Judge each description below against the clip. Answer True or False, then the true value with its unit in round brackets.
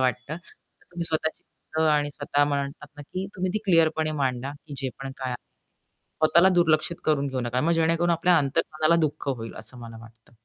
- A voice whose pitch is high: False (150 Hz)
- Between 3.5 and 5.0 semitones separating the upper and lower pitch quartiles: True (3.8 semitones)